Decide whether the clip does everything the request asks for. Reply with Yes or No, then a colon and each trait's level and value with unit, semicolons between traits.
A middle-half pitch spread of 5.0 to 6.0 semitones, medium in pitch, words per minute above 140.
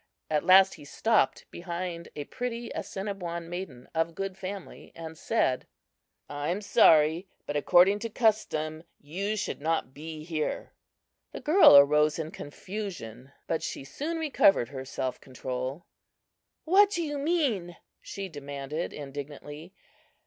No: wide, 5.5 semitones; medium, 170 Hz; slow, 135 wpm